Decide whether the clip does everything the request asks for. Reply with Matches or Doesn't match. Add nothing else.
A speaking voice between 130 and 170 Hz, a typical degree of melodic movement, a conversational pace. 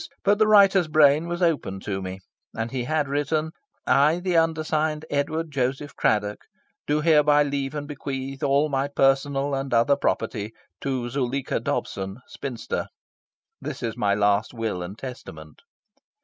Matches